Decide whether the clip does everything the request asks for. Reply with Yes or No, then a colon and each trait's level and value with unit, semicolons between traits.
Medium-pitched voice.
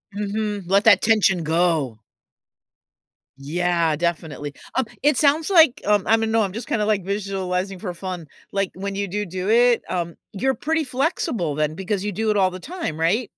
No: high, 195 Hz